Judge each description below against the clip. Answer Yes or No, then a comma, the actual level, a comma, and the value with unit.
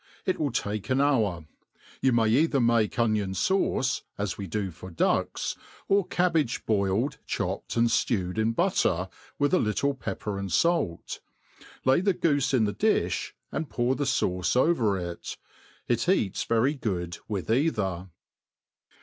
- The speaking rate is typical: Yes, average, 150 wpm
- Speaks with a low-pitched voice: Yes, low, 115 Hz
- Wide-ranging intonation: Yes, wide, 6.3 semitones